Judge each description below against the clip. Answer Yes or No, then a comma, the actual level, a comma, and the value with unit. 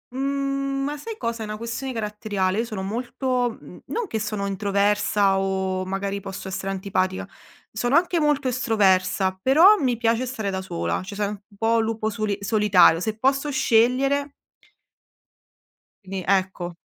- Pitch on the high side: Yes, high, 215 Hz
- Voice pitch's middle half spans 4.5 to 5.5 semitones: Yes, average, 4.8 semitones